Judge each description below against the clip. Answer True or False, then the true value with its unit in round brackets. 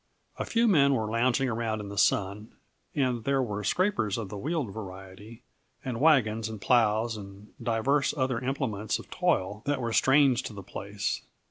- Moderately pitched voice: False (115 Hz)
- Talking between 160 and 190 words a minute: True (170 wpm)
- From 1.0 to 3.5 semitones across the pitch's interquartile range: False (4.2 semitones)